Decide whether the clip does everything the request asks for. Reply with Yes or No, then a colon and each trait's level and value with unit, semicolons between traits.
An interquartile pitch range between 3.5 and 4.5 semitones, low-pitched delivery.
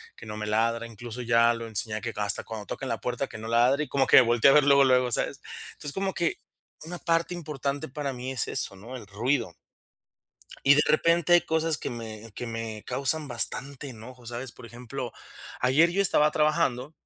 Yes: average, 4.0 semitones; low, 125 Hz